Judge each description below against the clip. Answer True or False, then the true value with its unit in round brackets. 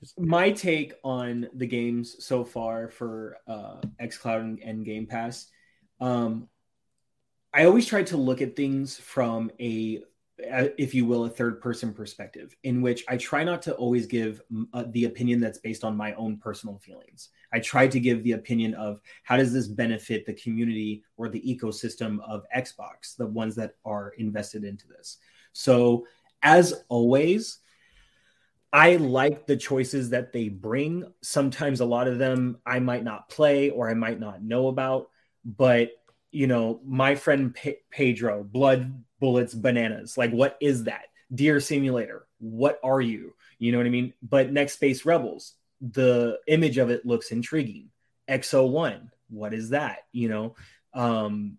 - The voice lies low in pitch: True (120 Hz)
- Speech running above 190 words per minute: False (160 wpm)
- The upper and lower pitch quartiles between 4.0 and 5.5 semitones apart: False (2.9 semitones)